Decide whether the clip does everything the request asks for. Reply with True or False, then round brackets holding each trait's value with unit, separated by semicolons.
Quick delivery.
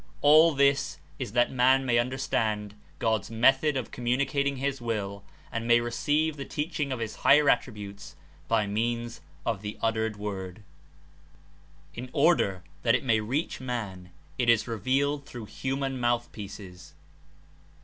False (150 wpm)